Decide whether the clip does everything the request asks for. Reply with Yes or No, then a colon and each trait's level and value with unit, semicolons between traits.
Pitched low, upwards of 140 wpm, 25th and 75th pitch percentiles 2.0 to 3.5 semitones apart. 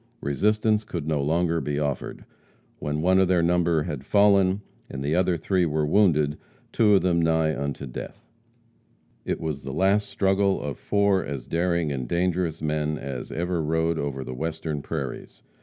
No: very low, 80 Hz; average, 170 wpm; average, 4.0 semitones